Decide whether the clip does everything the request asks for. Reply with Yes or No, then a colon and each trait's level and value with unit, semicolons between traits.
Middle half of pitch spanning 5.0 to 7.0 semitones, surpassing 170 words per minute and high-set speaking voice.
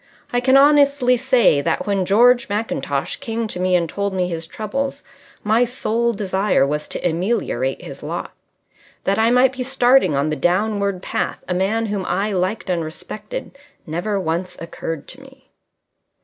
No: wide, 5.5 semitones; average, 165 wpm; high, 210 Hz